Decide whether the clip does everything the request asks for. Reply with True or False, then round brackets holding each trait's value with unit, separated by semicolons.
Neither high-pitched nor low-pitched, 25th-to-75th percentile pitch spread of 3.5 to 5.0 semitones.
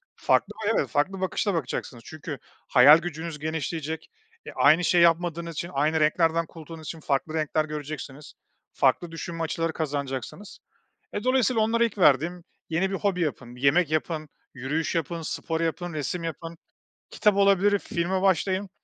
False (165 Hz; 2.9 semitones)